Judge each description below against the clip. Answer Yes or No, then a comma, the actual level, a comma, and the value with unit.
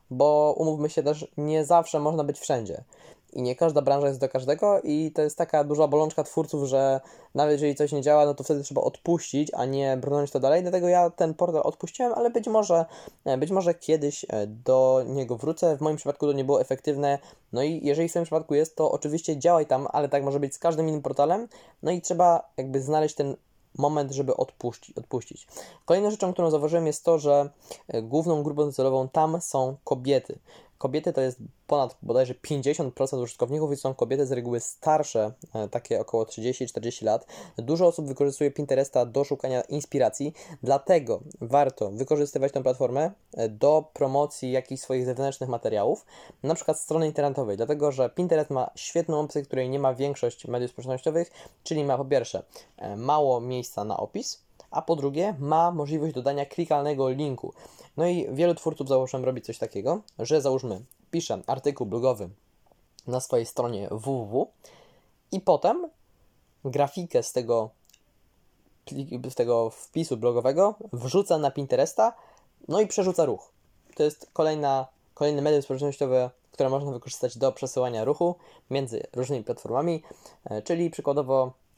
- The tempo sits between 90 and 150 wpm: No, fast, 160 wpm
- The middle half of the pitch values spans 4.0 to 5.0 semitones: No, average, 3.3 semitones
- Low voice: No, medium, 145 Hz